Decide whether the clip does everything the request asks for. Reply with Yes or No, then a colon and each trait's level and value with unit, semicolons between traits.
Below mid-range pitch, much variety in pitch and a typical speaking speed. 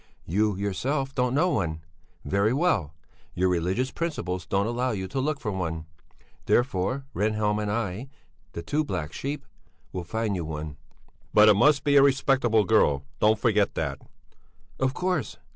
Yes: low, 105 Hz; wide, 6.5 semitones; average, 160 wpm